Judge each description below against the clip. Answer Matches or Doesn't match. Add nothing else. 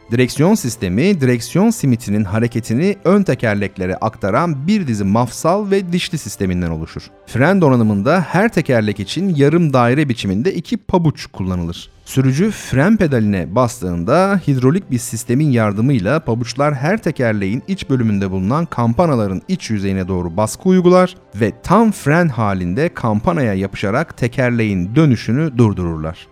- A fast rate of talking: Doesn't match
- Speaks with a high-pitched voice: Doesn't match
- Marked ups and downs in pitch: Matches